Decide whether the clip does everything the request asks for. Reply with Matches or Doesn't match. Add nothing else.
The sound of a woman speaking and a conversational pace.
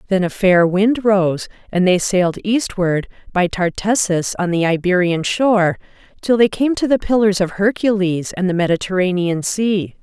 Matches